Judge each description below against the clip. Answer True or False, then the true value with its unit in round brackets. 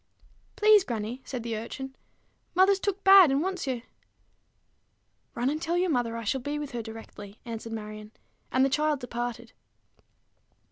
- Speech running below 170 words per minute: True (155 wpm)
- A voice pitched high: True (255 Hz)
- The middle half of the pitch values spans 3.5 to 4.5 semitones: False (5.3 semitones)